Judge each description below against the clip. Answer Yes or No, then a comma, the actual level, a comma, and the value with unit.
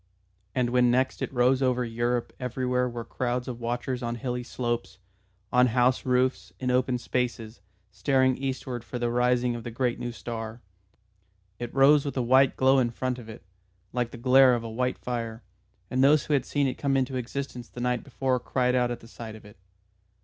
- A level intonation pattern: Yes, narrow, 1.4 semitones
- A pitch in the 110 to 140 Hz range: Yes, low, 125 Hz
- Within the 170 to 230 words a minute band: Yes, average, 200 wpm